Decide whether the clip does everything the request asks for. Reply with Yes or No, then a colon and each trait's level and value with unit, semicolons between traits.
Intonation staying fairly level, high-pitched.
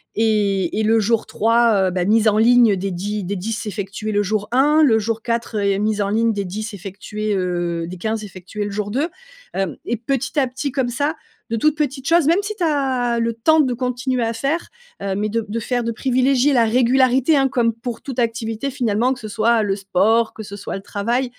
No: average, 3.7 semitones; high, 225 Hz